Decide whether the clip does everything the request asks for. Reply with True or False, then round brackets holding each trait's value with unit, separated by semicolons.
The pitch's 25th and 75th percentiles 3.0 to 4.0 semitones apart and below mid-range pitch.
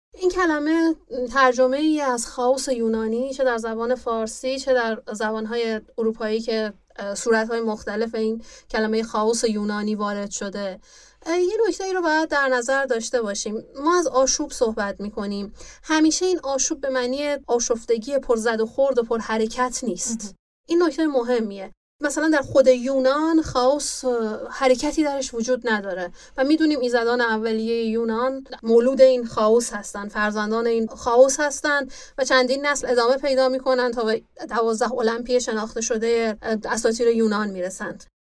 False (3.3 semitones; 240 Hz)